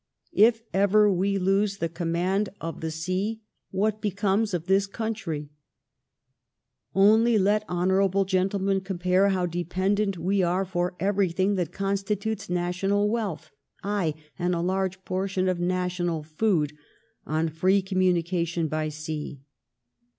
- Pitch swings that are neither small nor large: No, narrow, 2.3 semitones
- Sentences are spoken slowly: Yes, slow, 130 wpm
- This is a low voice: No, high, 190 Hz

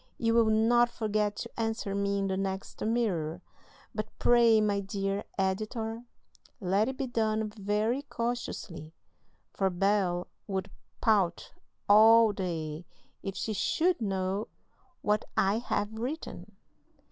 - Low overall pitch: No, high, 210 Hz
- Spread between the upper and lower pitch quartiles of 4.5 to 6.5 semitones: No, average, 2.7 semitones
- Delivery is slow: Yes, slow, 125 wpm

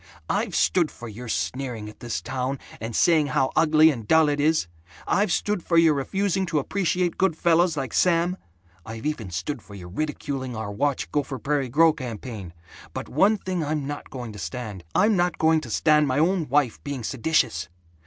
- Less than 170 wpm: No, average, 190 wpm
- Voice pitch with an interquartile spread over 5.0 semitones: Yes, wide, 5.4 semitones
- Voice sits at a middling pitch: Yes, medium, 145 Hz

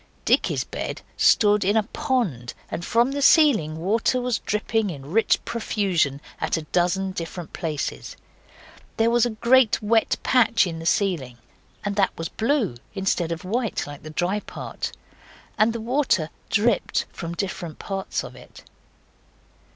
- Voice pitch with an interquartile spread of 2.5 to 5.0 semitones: No, wide, 5.6 semitones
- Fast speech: No, average, 150 wpm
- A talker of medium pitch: No, high, 200 Hz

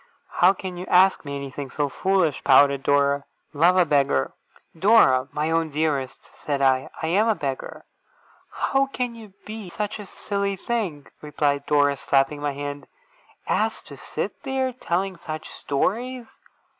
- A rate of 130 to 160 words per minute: Yes, average, 155 wpm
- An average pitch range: No, wide, 5.8 semitones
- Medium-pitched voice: Yes, medium, 155 Hz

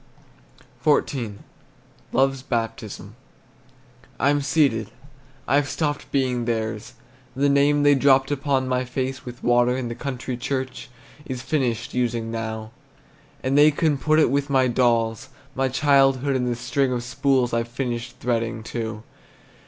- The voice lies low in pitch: Yes, low, 130 Hz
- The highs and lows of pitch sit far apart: No, average, 2.7 semitones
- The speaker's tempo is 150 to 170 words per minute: No, slow, 135 wpm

